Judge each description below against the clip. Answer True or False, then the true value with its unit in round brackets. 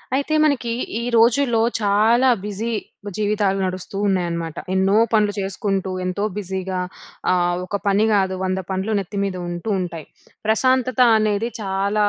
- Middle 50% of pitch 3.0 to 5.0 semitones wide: False (2.6 semitones)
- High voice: True (200 Hz)